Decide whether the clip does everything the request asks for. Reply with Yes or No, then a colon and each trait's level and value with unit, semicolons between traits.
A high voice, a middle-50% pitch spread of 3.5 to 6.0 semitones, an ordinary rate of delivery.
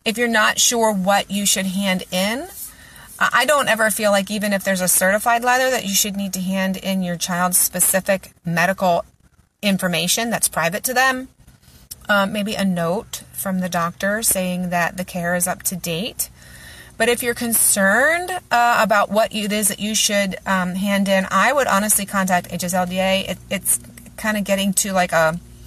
No: high, 195 Hz; average, 2.9 semitones; average, 185 wpm